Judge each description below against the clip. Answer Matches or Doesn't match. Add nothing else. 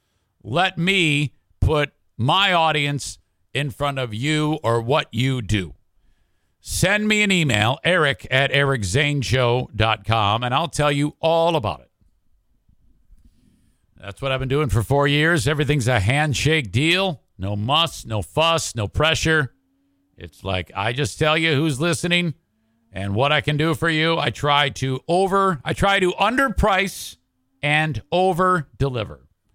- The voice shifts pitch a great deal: Matches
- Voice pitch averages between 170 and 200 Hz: Doesn't match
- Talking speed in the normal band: Matches